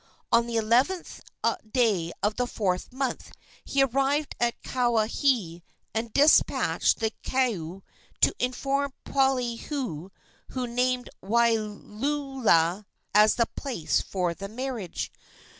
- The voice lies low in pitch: No, high, 235 Hz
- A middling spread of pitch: Yes, average, 4.1 semitones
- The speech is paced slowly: Yes, slow, 110 wpm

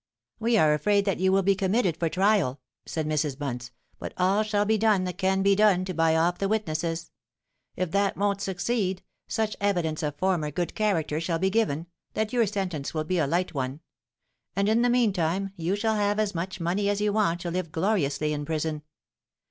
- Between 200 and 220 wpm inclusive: Yes, fast, 205 wpm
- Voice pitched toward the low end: No, medium, 185 Hz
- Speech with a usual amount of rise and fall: Yes, average, 4.1 semitones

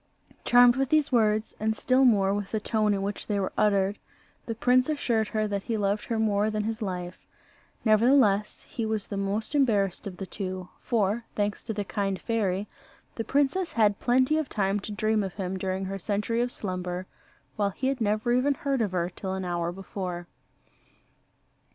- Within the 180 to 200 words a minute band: Yes, average, 190 wpm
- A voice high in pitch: Yes, high, 210 Hz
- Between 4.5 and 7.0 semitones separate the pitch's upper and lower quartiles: No, average, 3.0 semitones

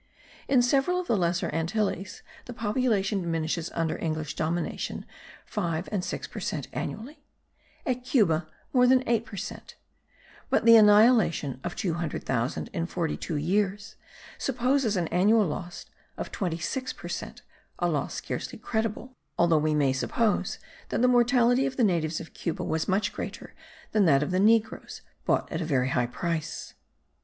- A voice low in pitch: No, high, 190 Hz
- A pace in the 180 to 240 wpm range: No, average, 160 wpm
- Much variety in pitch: Yes, wide, 6.0 semitones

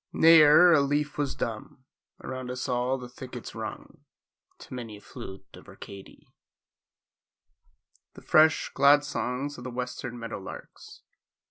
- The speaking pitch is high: No, low, 130 Hz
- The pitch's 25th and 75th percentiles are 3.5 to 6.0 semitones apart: No, average, 3.0 semitones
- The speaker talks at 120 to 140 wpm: Yes, slow, 135 wpm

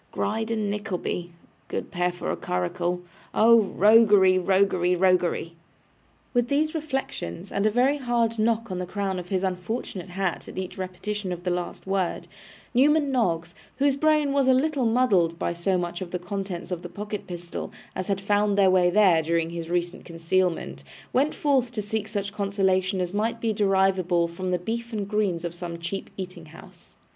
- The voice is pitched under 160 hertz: No, high, 195 Hz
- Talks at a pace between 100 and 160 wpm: No, average, 180 wpm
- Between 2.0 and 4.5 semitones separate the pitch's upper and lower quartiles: Yes, average, 3.9 semitones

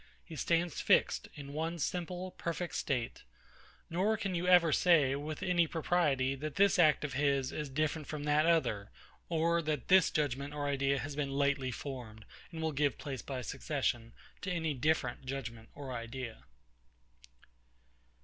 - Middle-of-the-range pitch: Yes, medium, 145 Hz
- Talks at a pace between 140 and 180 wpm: Yes, average, 160 wpm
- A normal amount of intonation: Yes, average, 3.8 semitones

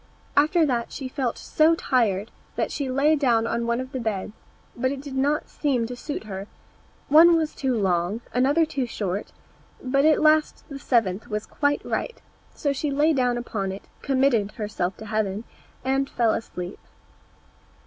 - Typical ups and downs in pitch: Yes, average, 4.7 semitones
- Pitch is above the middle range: Yes, very high, 255 Hz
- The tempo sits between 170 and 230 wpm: Yes, average, 175 wpm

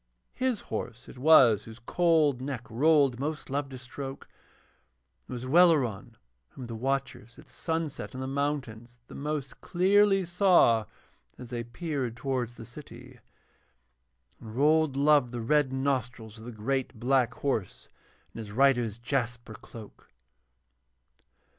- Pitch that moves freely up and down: No, average, 3.9 semitones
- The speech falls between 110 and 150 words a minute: Yes, average, 140 wpm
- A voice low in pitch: Yes, low, 130 Hz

